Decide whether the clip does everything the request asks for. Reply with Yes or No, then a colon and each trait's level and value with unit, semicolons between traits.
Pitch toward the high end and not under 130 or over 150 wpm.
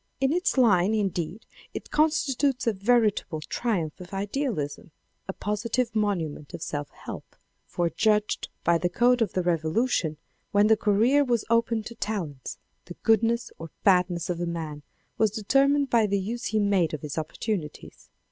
No: high, 205 Hz; average, 165 wpm